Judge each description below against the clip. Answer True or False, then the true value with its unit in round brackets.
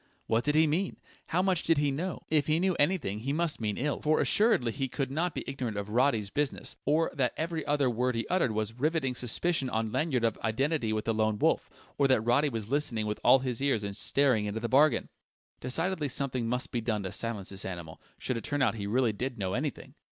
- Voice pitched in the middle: False (130 Hz)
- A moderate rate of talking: False (230 wpm)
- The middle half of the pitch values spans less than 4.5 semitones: False (5.0 semitones)